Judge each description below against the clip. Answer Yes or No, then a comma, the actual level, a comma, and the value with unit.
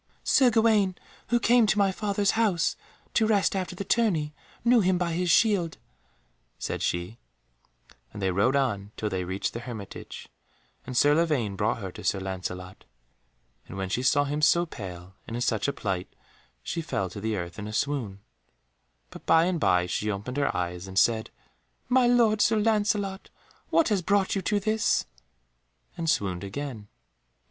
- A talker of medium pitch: Yes, medium, 145 Hz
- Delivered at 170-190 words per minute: Yes, average, 175 wpm